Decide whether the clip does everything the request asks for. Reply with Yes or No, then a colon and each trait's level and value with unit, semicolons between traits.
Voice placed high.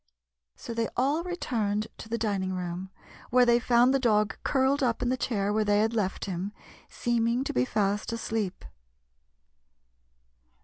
Yes: high, 225 Hz